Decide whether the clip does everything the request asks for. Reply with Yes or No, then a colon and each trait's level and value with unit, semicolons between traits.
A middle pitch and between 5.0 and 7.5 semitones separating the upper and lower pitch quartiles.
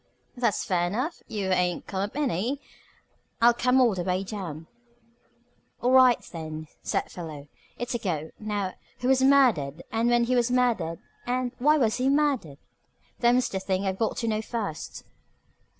No: high, 220 Hz; wide, 5.6 semitones